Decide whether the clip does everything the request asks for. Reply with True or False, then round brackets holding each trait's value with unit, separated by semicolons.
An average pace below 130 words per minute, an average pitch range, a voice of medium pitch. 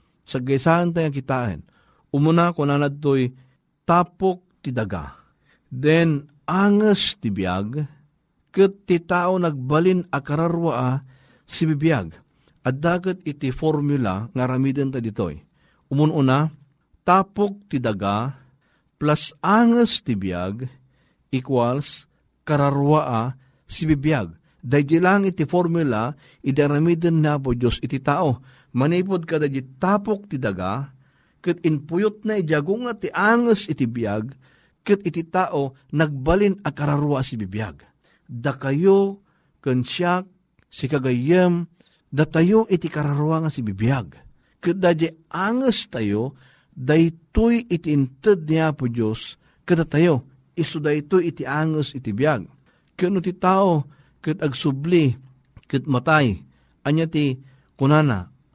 True (115 wpm; 4.5 semitones; 150 Hz)